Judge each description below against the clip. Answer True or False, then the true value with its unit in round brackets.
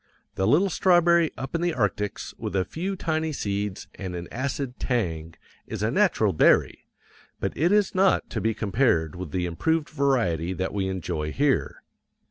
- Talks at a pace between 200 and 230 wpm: False (170 wpm)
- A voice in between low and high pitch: False (115 Hz)